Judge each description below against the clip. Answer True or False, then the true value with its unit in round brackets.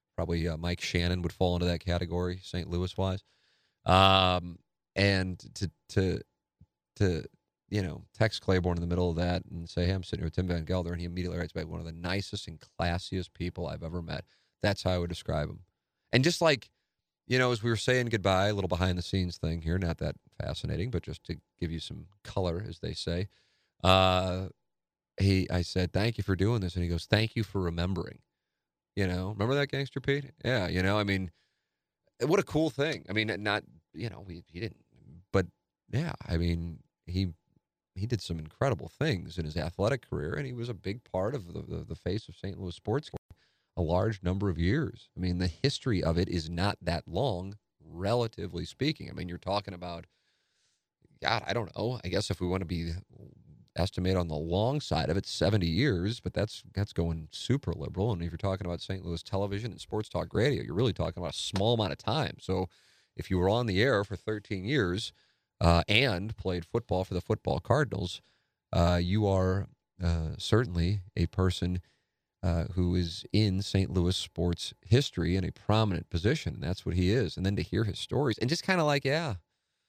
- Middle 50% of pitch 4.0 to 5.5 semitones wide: False (3.4 semitones)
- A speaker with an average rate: False (210 wpm)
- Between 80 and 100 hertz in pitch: True (95 Hz)